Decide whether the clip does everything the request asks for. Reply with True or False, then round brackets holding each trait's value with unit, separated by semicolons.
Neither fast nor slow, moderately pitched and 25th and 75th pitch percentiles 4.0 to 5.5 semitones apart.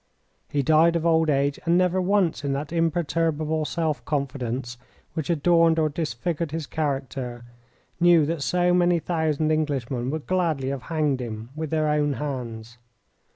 False (155 wpm; 155 Hz; 3.4 semitones)